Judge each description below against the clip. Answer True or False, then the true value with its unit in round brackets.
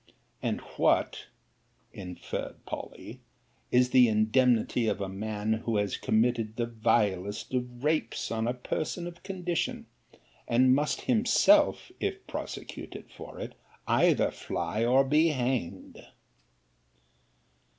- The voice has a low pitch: True (120 Hz)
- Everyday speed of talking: False (115 wpm)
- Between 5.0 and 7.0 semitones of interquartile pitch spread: True (5.4 semitones)